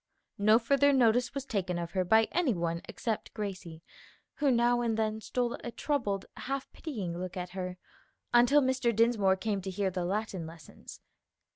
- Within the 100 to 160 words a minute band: No, average, 170 wpm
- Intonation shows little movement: No, average, 4.8 semitones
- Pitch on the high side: Yes, high, 215 Hz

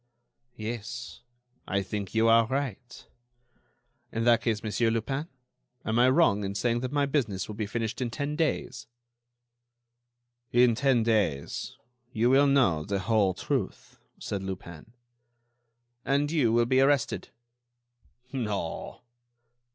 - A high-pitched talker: No, low, 115 Hz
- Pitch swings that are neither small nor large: Yes, average, 4.0 semitones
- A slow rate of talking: Yes, slow, 130 wpm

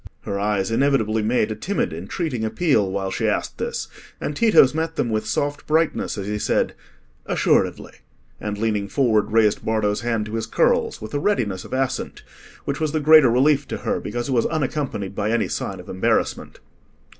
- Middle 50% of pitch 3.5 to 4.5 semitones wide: No, average, 5.2 semitones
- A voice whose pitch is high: No, low, 115 Hz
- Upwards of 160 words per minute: Yes, average, 185 wpm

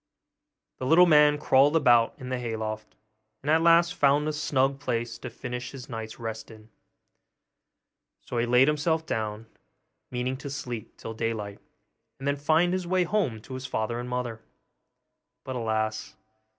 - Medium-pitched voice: No, low, 130 Hz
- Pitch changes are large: No, average, 4.5 semitones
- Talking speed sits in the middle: Yes, average, 165 wpm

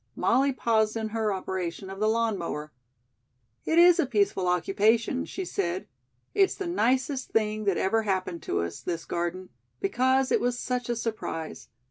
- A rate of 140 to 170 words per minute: Yes, average, 165 wpm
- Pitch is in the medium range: No, high, 215 Hz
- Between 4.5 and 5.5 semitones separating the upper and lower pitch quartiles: Yes, average, 5.0 semitones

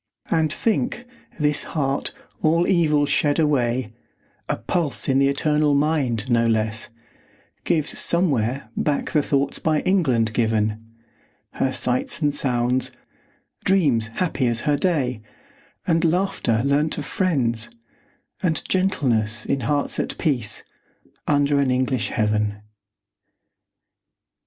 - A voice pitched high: No, medium, 140 Hz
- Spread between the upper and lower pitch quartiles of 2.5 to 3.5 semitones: No, average, 4.8 semitones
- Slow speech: Yes, slow, 120 wpm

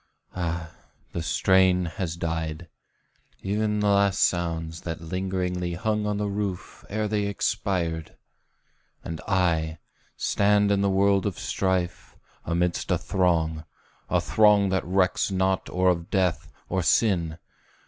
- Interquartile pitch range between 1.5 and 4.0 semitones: Yes, average, 3.0 semitones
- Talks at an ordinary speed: No, slow, 130 wpm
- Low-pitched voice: Yes, very low, 90 Hz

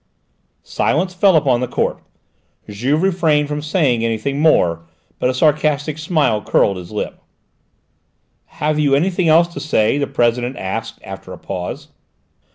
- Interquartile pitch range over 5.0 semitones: Yes, wide, 5.5 semitones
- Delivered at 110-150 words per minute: Yes, average, 145 wpm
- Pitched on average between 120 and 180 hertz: Yes, medium, 140 Hz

